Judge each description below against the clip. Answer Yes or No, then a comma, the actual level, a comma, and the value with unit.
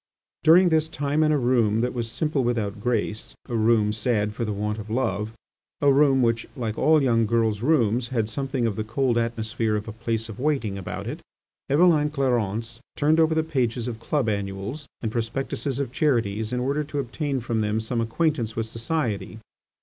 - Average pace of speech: Yes, average, 190 wpm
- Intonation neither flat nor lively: Yes, average, 4.2 semitones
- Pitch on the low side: Yes, low, 120 Hz